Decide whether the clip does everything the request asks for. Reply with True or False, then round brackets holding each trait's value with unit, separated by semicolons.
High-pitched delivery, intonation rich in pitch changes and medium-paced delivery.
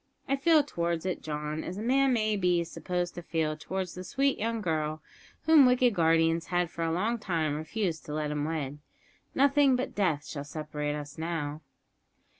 False (170 Hz; 6.1 semitones; 185 wpm)